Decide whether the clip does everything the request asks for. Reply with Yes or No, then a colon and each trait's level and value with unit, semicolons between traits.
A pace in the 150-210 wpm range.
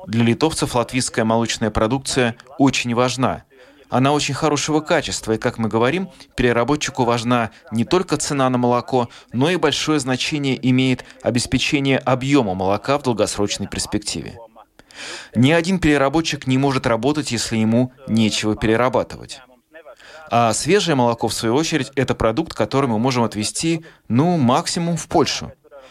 No: average, 135 wpm